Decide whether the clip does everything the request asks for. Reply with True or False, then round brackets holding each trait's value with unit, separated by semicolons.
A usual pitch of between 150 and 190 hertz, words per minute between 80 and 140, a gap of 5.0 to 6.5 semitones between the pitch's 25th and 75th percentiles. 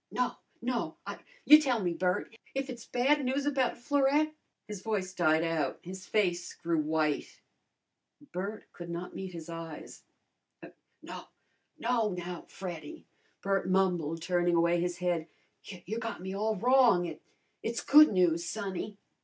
False (185 Hz; 155 wpm; 5.5 semitones)